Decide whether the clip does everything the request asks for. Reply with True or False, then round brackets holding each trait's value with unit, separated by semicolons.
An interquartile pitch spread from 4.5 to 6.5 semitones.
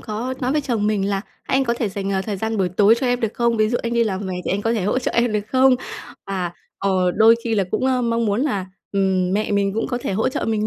False (3.1 semitones)